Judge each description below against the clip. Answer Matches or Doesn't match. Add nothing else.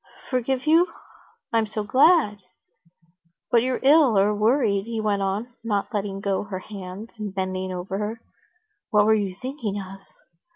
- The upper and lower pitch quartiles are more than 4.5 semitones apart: Doesn't match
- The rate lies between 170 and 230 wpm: Doesn't match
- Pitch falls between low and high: Doesn't match